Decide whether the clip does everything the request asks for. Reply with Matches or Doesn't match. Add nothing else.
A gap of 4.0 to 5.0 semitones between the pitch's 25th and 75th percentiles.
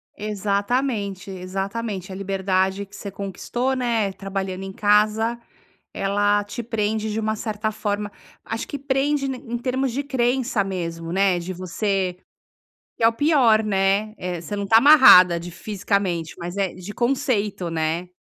Doesn't match